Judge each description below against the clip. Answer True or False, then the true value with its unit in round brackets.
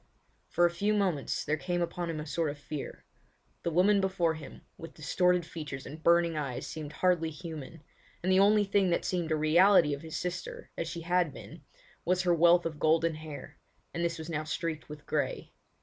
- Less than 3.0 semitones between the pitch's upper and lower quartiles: True (2.5 semitones)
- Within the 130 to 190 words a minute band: False (200 wpm)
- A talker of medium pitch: True (165 Hz)